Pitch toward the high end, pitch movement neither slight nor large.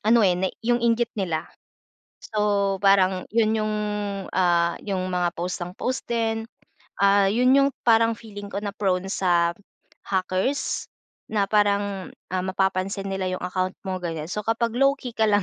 Yes: high, 200 Hz; average, 3.2 semitones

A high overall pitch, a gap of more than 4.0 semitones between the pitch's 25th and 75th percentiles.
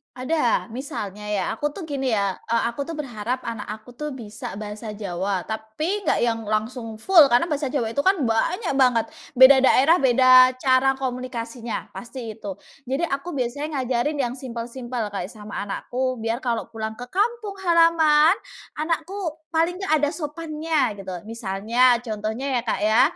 Yes: very high, 255 Hz; average, 5.0 semitones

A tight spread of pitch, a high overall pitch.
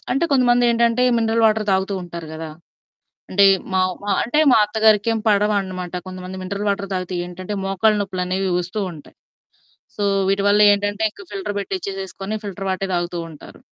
Yes: narrow, 2.3 semitones; high, 200 Hz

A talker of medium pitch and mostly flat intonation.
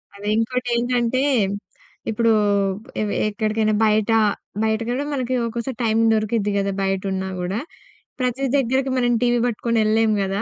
No: high, 225 Hz; narrow, 2.3 semitones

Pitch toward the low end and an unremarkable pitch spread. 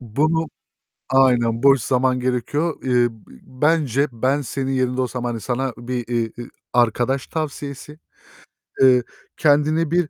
Yes: low, 130 Hz; average, 3.1 semitones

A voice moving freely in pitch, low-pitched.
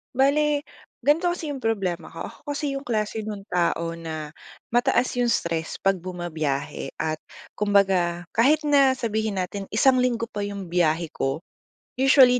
No: wide, 7.0 semitones; high, 210 Hz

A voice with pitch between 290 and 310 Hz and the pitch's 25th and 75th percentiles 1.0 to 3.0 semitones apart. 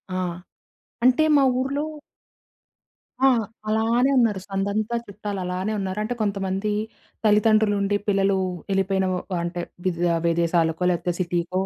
No: high, 195 Hz; average, 2.7 semitones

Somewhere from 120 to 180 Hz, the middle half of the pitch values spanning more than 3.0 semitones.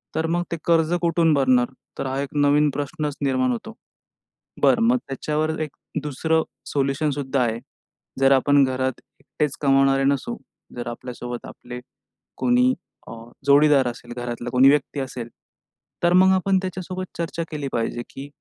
Yes: medium, 140 Hz; average, 3.6 semitones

